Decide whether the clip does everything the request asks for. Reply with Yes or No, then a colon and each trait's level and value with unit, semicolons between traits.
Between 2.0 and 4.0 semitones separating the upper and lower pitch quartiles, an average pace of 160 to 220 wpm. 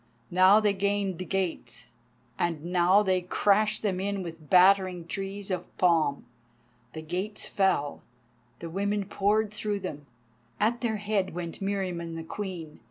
No: average, 2.9 semitones; average, 145 wpm